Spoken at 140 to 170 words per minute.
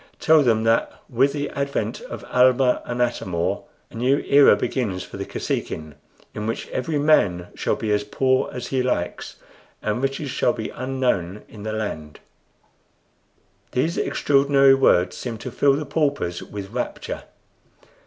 Yes: average, 155 wpm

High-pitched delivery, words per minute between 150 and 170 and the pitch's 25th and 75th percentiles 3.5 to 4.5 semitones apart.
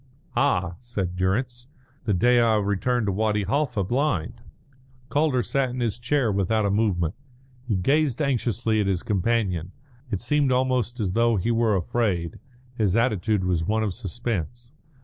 No: low, 110 Hz; average, 155 wpm; average, 4.1 semitones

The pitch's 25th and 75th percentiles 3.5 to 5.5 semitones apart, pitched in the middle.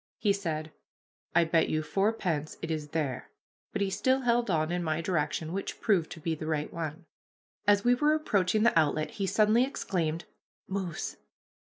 Yes: average, 4.7 semitones; medium, 175 Hz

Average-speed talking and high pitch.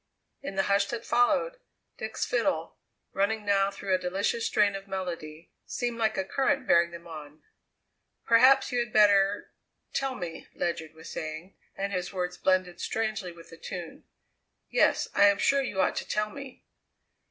Yes: average, 165 wpm; high, 195 Hz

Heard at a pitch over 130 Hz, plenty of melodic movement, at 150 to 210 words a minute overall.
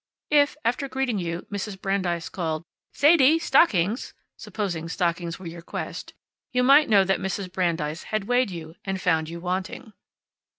Yes: high, 190 Hz; wide, 6.4 semitones; average, 155 wpm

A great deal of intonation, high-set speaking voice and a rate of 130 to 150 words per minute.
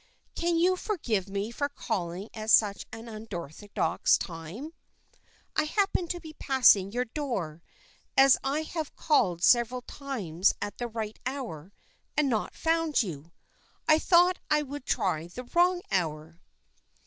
Yes: wide, 8.0 semitones; high, 240 Hz; average, 145 wpm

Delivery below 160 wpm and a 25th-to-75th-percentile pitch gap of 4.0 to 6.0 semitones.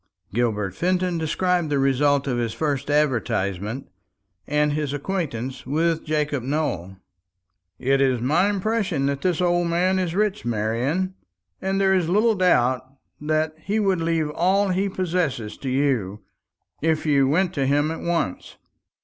Yes: average, 150 wpm; wide, 5.4 semitones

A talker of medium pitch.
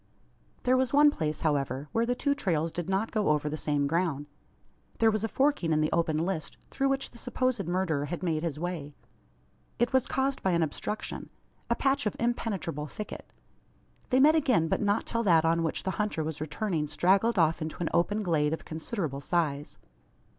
Yes: medium, 175 Hz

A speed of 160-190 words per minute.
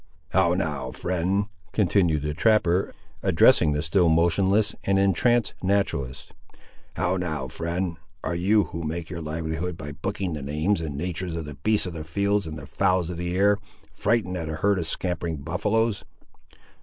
Yes: average, 170 wpm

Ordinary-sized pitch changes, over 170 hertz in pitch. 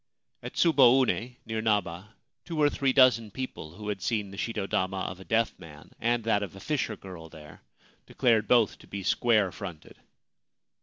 No: average, 4.1 semitones; low, 105 Hz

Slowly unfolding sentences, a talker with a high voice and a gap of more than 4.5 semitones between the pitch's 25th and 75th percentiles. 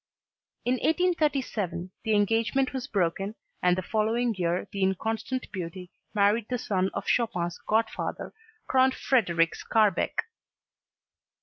Yes: slow, 115 wpm; high, 215 Hz; average, 4.9 semitones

